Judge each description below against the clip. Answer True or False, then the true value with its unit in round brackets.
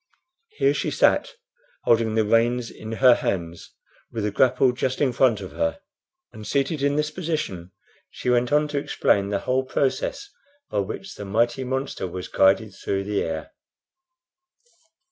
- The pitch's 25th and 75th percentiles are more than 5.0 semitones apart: True (5.5 semitones)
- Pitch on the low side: True (120 Hz)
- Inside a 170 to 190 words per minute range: False (160 wpm)